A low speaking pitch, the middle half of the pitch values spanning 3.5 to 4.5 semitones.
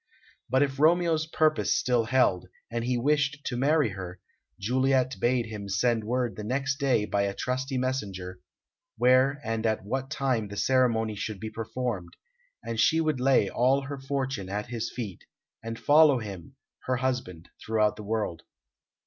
Yes: low, 125 Hz; average, 4.0 semitones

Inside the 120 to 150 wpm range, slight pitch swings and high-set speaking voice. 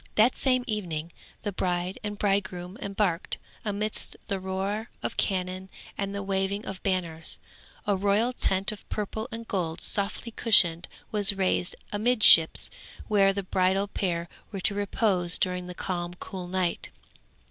Yes: average, 145 wpm; narrow, 2.3 semitones; high, 195 Hz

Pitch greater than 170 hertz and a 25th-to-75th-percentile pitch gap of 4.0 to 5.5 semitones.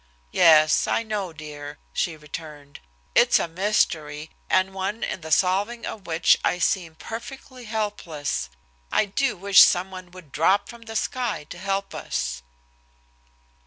Yes: medium, 185 Hz; average, 4.9 semitones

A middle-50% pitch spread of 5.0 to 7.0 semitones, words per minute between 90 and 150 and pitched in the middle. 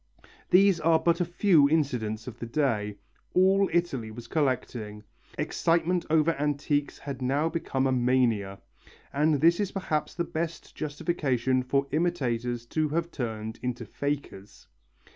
Yes: wide, 5.4 semitones; average, 140 wpm; medium, 145 Hz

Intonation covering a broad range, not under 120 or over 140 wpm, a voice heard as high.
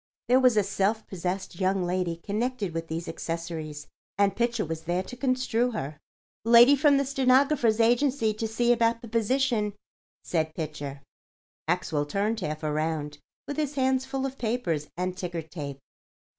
No: wide, 7.0 semitones; average, 155 wpm; high, 205 Hz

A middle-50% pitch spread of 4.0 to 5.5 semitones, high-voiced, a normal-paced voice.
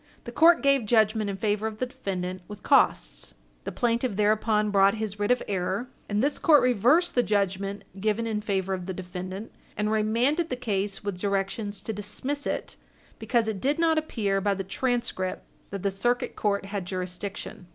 No: average, 3.4 semitones; high, 210 Hz; average, 185 wpm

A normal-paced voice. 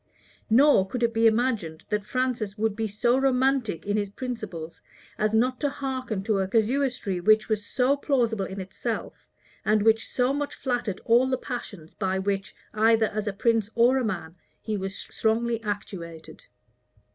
Yes: average, 170 wpm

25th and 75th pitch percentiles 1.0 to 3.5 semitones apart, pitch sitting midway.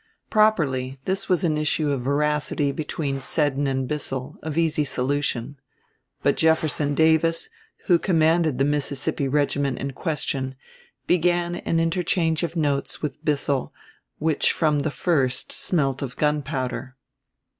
Yes: average, 2.9 semitones; medium, 150 Hz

